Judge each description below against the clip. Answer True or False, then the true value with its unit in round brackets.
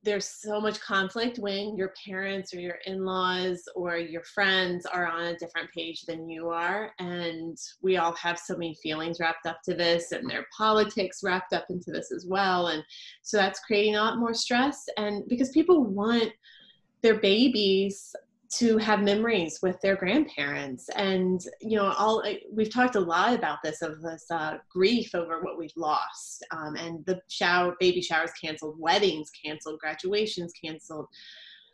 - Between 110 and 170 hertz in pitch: False (185 Hz)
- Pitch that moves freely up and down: False (3.8 semitones)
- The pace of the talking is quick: False (170 wpm)